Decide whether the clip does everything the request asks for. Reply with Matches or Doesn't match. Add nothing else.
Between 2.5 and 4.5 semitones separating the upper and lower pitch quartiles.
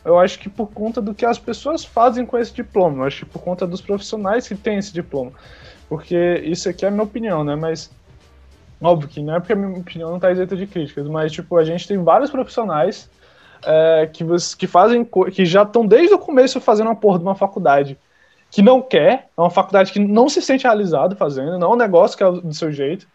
Doesn't match